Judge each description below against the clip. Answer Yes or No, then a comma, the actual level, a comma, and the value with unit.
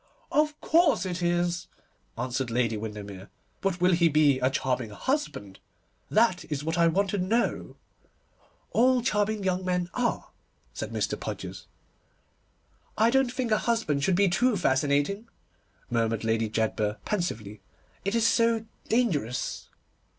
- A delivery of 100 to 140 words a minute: Yes, slow, 135 wpm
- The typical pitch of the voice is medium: Yes, medium, 175 Hz